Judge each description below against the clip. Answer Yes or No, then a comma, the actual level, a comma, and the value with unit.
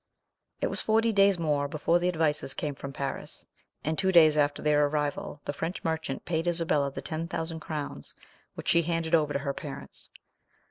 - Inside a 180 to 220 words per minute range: Yes, average, 185 wpm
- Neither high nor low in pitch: Yes, medium, 155 Hz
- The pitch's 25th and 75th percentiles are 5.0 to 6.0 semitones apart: No, narrow, 2.6 semitones